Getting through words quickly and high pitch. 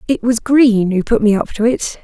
Yes: fast, 265 wpm; high, 225 Hz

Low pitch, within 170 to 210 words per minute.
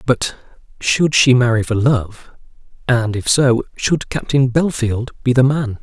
No: low, 125 Hz; average, 155 wpm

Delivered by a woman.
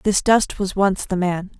Yes: female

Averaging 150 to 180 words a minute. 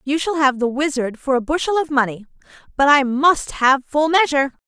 No: fast, 205 wpm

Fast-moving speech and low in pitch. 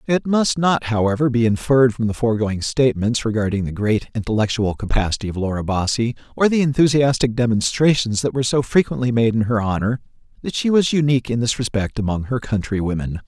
No: average, 180 wpm; low, 120 Hz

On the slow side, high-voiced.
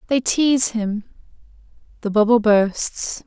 Yes: slow, 110 wpm; high, 225 Hz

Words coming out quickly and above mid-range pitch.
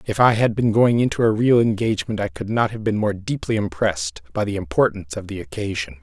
No: fast, 230 wpm; low, 110 Hz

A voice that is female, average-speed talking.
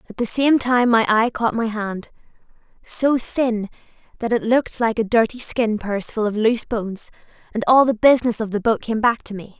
No: female; fast, 215 wpm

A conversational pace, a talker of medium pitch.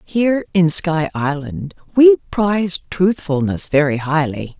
No: slow, 120 wpm; medium, 165 Hz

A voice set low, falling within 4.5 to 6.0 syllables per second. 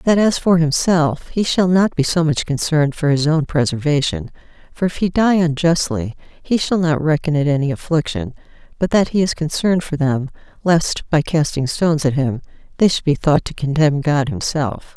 No: medium, 155 Hz; 5.0 syllables/s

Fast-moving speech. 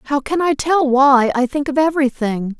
Yes: fast, 230 wpm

